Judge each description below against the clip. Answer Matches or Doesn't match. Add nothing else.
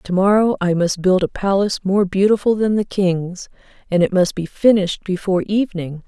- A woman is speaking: Matches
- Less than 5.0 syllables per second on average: Doesn't match